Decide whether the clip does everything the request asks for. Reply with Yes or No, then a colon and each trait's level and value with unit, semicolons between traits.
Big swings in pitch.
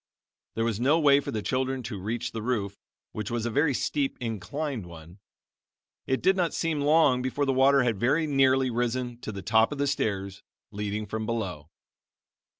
No: average, 4.5 semitones